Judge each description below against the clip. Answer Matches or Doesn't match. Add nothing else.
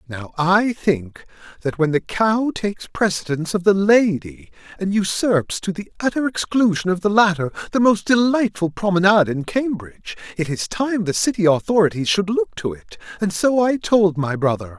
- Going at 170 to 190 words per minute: Matches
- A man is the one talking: Matches